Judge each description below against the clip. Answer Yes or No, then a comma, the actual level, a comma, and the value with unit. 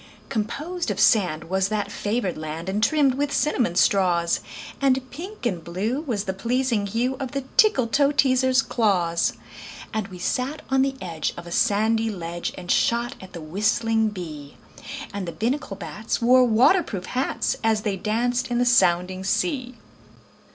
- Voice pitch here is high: Yes, high, 220 Hz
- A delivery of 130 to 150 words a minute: No, average, 160 wpm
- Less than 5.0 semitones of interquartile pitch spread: No, wide, 5.5 semitones